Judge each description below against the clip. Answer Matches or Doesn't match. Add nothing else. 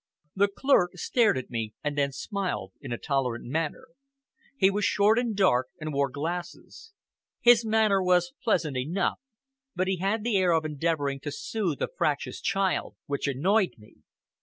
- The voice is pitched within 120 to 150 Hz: Doesn't match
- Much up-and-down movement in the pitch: Matches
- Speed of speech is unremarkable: Matches